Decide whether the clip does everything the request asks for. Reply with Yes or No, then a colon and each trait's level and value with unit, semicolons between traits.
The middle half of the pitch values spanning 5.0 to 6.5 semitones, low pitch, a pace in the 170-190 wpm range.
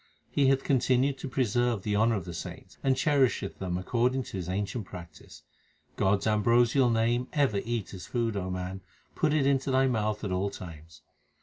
Yes: average, 5.3 semitones; low, 115 Hz; average, 185 wpm